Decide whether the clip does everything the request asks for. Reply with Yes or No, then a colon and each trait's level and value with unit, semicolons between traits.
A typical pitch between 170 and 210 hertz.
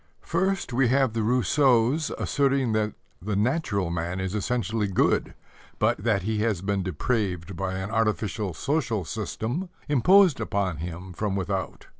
No: low, 110 Hz